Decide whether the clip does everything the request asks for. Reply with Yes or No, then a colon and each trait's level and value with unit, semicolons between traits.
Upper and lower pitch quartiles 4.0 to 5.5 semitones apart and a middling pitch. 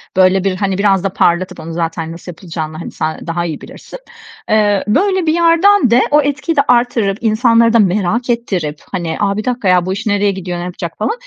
No: average, 5.2 semitones; high, 200 Hz